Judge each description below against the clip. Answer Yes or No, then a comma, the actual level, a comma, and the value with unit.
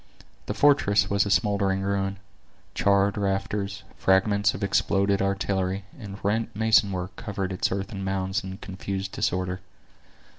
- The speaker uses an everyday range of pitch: No, narrow, 1.0 semitones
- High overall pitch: No, low, 100 Hz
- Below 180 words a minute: Yes, slow, 135 wpm